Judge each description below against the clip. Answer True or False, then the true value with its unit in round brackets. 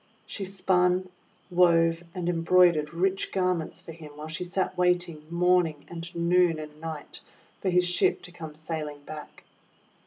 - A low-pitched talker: False (170 Hz)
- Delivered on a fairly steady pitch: True (2.2 semitones)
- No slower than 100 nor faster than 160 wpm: True (150 wpm)